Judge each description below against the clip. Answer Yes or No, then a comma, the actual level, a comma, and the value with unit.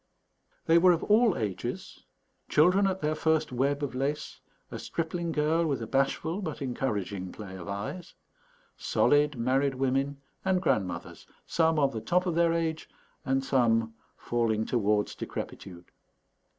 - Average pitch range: No, wide, 6.2 semitones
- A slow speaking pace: No, average, 145 wpm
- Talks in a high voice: No, medium, 140 Hz